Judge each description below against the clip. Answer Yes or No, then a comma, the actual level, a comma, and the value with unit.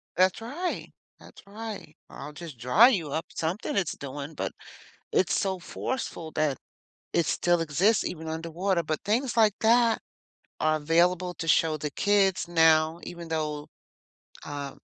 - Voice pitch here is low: No, medium, 170 Hz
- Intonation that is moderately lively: Yes, average, 4.2 semitones